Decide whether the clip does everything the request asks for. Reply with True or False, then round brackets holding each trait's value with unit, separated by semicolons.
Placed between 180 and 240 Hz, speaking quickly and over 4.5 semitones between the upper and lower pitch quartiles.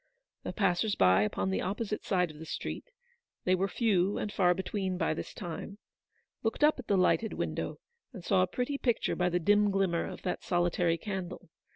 False (190 Hz; 210 wpm; 2.9 semitones)